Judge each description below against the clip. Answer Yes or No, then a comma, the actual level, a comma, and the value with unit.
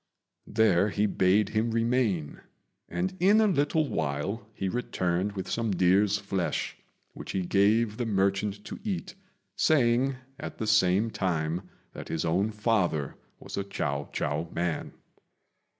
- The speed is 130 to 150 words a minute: Yes, average, 140 wpm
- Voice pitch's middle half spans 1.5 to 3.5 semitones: No, average, 4.1 semitones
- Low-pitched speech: Yes, low, 100 Hz